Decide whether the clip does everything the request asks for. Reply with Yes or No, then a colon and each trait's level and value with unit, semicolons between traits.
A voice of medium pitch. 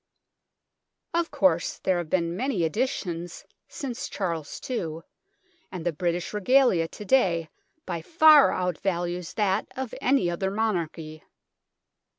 Yes: medium, 180 Hz